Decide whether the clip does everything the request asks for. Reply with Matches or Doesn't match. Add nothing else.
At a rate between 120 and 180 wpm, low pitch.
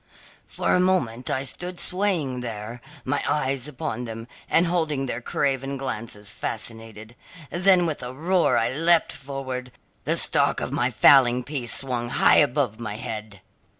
Matches